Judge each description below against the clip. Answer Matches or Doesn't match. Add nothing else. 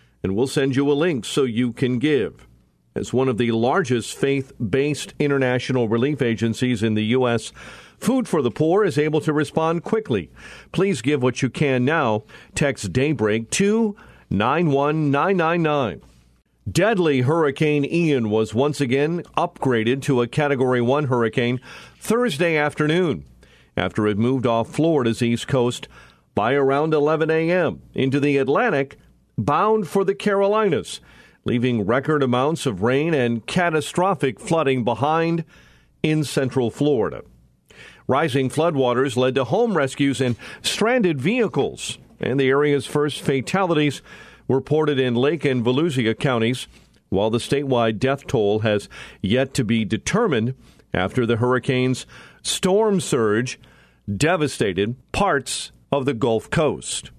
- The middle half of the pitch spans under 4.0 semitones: Doesn't match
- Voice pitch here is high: Doesn't match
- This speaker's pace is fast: Doesn't match